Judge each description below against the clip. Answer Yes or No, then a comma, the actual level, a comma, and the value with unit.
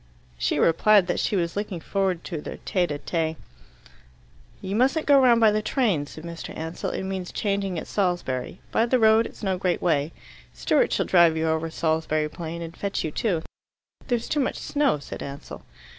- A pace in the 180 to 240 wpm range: Yes, average, 190 wpm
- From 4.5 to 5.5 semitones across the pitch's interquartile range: Yes, average, 4.8 semitones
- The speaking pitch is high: No, medium, 180 Hz